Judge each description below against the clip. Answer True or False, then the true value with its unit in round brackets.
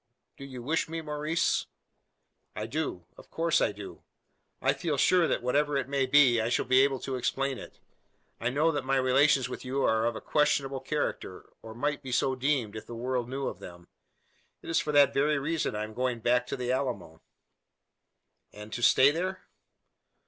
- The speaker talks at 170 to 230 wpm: True (195 wpm)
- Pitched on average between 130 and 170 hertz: True (135 Hz)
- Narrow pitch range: False (3.4 semitones)